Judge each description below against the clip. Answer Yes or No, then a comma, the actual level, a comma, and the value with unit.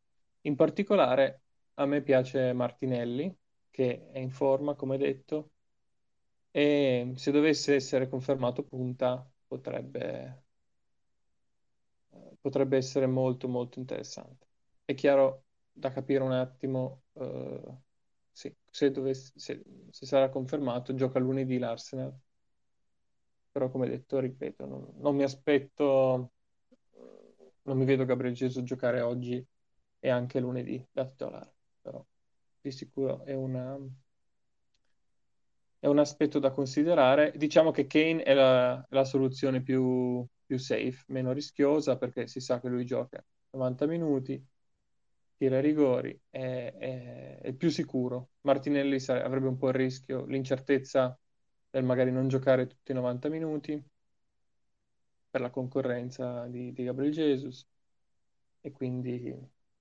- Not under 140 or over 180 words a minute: No, average, 125 wpm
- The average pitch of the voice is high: No, low, 130 Hz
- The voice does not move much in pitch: Yes, narrow, 1.6 semitones